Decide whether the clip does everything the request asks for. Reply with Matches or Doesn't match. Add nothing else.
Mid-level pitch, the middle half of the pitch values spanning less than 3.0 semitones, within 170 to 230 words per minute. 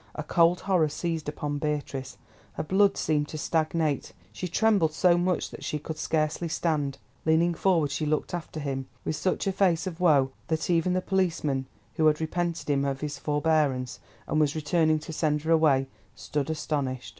Matches